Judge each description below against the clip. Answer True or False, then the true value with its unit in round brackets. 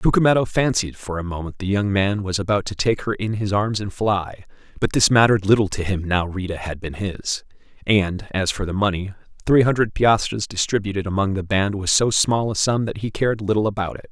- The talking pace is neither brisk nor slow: False (220 wpm)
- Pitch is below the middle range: True (100 Hz)